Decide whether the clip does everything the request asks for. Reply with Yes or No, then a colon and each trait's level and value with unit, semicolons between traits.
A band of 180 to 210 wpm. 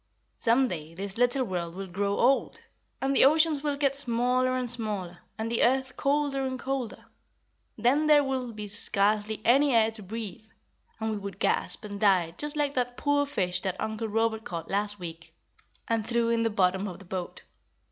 Yes: average, 190 wpm